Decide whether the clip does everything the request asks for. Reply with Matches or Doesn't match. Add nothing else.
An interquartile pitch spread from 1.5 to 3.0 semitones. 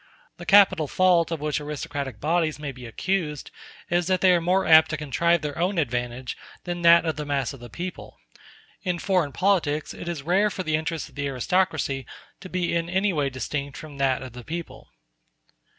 Doesn't match